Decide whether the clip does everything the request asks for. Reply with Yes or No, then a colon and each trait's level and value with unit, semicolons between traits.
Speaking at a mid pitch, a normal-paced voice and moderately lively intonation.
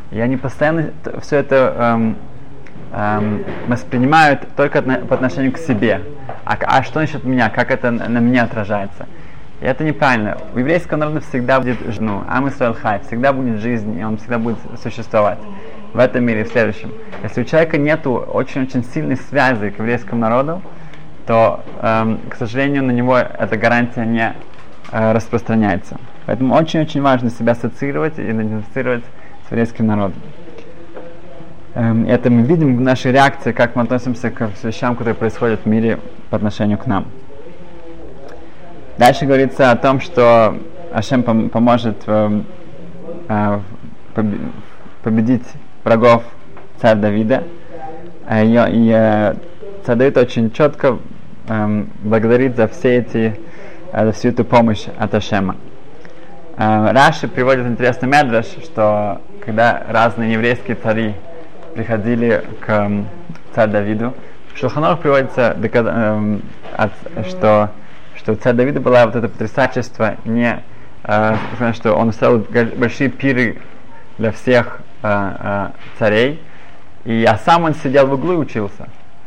No: low, 120 Hz; average, 125 wpm; average, 3.3 semitones